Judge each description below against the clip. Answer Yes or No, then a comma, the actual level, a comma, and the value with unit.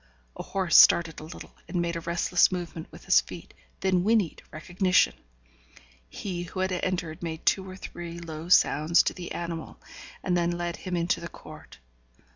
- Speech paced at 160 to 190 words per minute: Yes, average, 175 wpm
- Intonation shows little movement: Yes, narrow, 1.6 semitones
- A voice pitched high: No, medium, 175 Hz